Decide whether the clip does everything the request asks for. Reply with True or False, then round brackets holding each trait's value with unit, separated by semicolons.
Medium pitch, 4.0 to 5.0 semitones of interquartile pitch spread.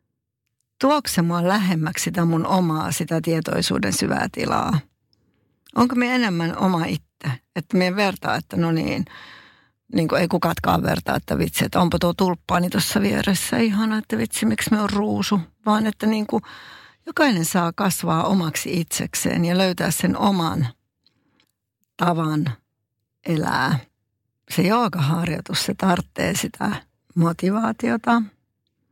True (175 Hz; 4.7 semitones)